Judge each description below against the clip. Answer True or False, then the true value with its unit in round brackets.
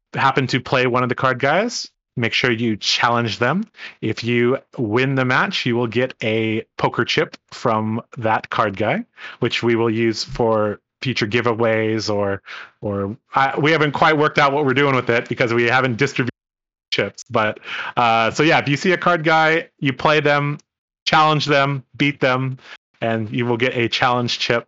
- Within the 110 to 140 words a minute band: False (185 wpm)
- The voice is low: True (125 Hz)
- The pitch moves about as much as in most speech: True (3.5 semitones)